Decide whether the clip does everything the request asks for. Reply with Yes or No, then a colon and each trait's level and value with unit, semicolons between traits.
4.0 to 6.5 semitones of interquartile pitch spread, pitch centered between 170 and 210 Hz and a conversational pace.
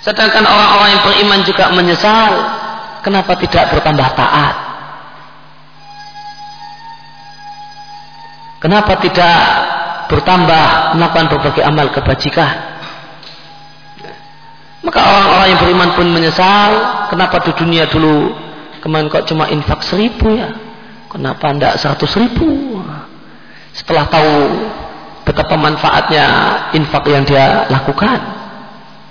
Yes: average, 5.3 semitones; medium, 185 Hz; average, 95 wpm